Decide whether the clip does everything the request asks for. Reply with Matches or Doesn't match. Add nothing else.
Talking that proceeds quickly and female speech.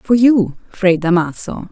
Doesn't match